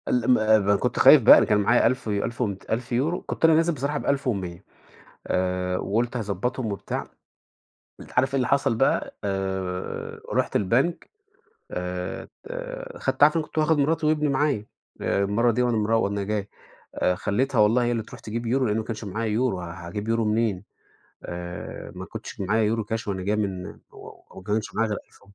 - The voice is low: Yes, low, 110 Hz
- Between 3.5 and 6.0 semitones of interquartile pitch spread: Yes, average, 4.2 semitones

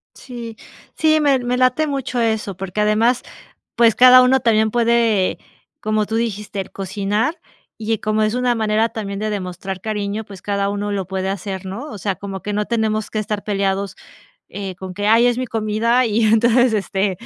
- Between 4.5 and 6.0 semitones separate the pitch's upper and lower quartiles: No, average, 2.8 semitones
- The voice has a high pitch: Yes, high, 215 Hz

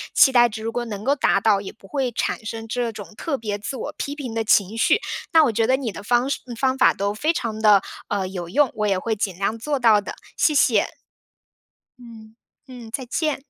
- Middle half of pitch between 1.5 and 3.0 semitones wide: No, average, 3.7 semitones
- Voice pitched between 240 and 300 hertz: No, high, 225 Hz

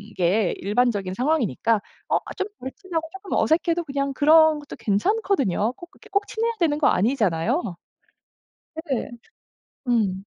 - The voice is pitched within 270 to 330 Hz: Yes, very high, 275 Hz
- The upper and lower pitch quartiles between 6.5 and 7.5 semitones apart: No, wide, 8.1 semitones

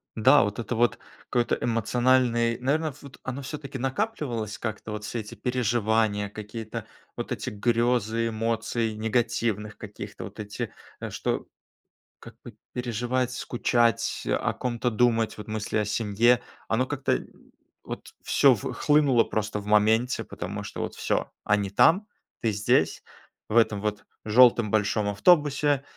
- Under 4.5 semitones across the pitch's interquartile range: Yes, average, 2.8 semitones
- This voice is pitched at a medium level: No, low, 115 Hz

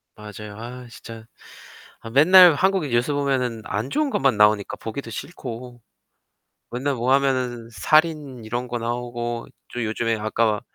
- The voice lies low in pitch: Yes, low, 120 Hz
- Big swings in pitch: No, average, 3.3 semitones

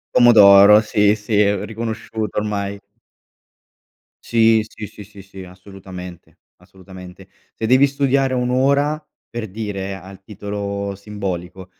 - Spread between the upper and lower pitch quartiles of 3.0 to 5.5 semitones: No, narrow, 2.6 semitones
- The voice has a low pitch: Yes, low, 105 Hz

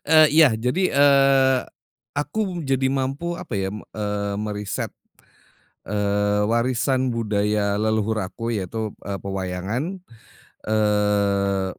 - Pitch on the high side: No, low, 110 Hz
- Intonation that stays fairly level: No, average, 4.7 semitones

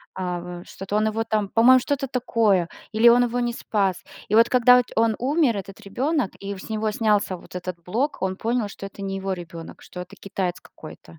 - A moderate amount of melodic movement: Yes, average, 4.0 semitones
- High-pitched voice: Yes, high, 210 Hz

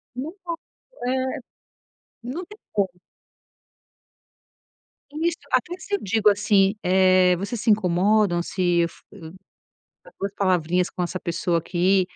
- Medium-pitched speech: No, high, 195 Hz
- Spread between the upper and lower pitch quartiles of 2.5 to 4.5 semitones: No, wide, 5.6 semitones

